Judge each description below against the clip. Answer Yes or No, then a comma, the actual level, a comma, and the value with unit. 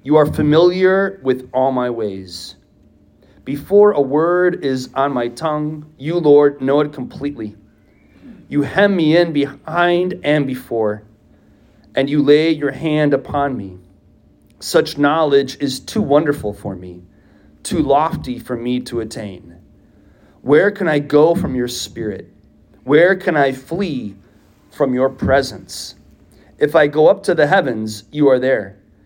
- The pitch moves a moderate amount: No, wide, 6.4 semitones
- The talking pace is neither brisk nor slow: Yes, average, 145 wpm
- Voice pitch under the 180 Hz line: Yes, low, 135 Hz